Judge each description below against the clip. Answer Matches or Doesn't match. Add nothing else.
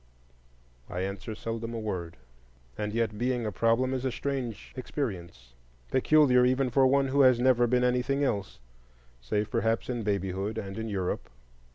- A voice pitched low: Matches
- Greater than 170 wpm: Doesn't match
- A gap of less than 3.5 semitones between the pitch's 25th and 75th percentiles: Doesn't match